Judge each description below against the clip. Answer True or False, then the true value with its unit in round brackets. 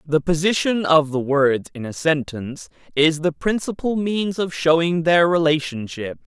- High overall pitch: False (160 Hz)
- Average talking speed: True (150 wpm)